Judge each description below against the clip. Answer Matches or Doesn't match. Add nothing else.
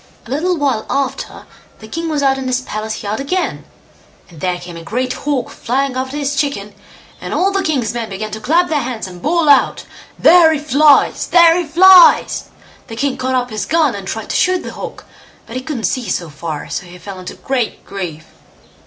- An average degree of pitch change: Doesn't match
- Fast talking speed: Matches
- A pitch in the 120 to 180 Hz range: Doesn't match